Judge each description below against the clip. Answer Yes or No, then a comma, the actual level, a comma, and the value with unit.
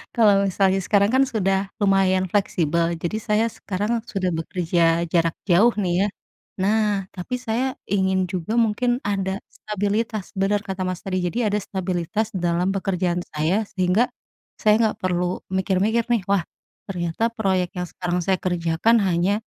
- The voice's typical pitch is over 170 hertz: Yes, high, 190 Hz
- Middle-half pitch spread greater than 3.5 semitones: No, average, 2.8 semitones